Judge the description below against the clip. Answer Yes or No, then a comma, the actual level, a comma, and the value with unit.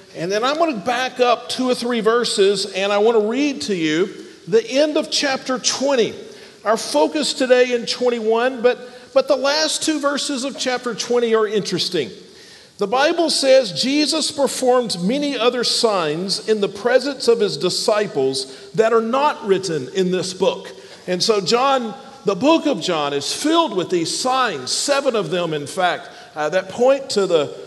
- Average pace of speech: Yes, average, 180 wpm